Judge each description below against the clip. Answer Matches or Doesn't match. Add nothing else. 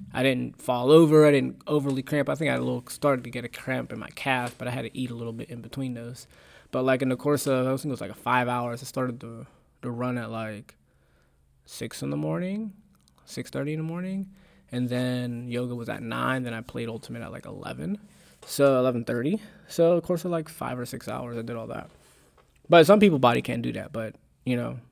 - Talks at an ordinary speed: Doesn't match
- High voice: Doesn't match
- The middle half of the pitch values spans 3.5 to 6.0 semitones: Matches